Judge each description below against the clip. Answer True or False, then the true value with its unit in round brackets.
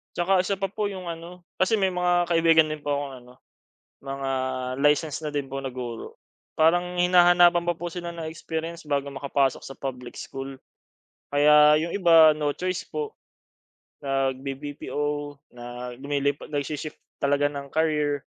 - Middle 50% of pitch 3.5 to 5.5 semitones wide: True (3.8 semitones)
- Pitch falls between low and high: True (150 Hz)